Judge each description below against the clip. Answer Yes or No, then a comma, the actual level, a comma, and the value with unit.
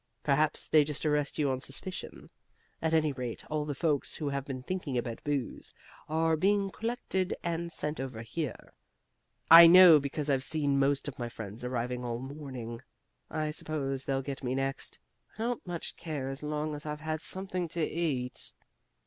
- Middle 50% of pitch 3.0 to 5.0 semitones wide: Yes, average, 3.3 semitones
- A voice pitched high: No, medium, 150 Hz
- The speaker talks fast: No, average, 175 wpm